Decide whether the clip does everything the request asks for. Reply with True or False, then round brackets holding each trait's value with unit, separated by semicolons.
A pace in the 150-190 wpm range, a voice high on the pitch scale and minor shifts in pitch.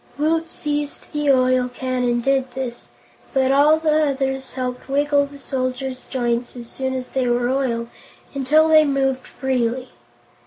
True (155 wpm; 265 Hz; 2.1 semitones)